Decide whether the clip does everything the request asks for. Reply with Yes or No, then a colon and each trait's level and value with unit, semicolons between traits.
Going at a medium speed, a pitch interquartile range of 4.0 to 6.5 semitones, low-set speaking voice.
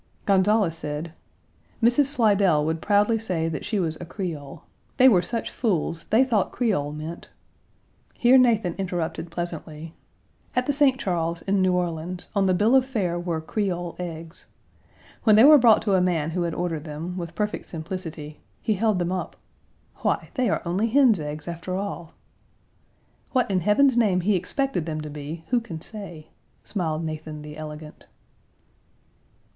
No: average, 165 wpm; average, 5.0 semitones; medium, 180 Hz